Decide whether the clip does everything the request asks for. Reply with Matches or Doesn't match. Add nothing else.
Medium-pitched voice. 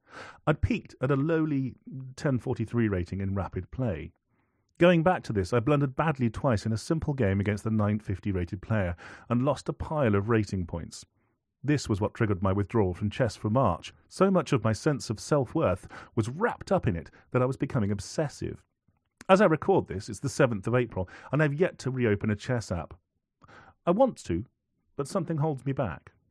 Doesn't match